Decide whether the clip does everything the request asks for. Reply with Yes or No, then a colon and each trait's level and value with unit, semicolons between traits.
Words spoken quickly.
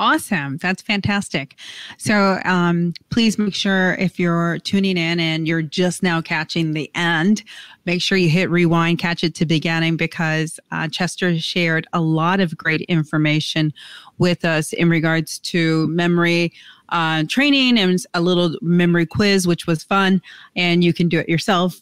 No: average, 160 wpm